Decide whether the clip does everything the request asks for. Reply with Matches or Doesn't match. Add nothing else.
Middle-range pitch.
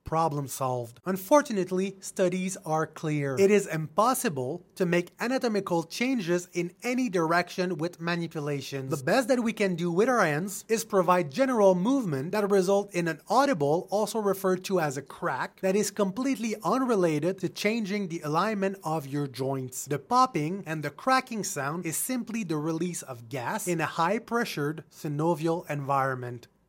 Matches